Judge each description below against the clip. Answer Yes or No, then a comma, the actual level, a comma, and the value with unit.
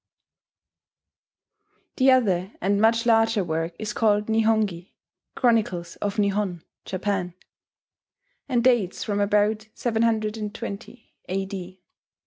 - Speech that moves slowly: Yes, slow, 100 wpm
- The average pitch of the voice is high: Yes, high, 210 Hz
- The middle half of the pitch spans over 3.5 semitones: No, average, 2.9 semitones